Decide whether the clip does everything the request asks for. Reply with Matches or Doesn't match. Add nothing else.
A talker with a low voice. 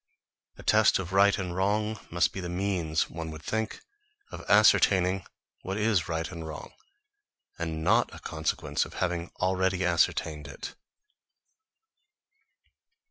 Matches